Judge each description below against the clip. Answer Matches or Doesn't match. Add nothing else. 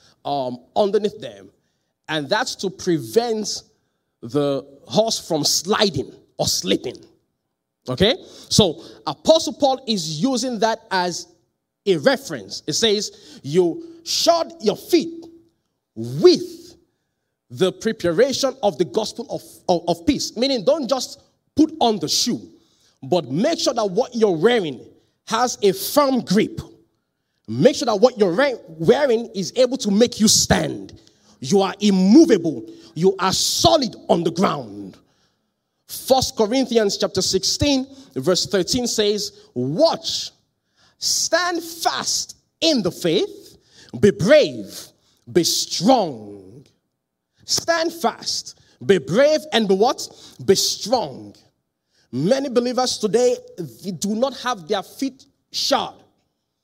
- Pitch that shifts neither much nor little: Doesn't match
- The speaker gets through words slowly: Matches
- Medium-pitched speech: Doesn't match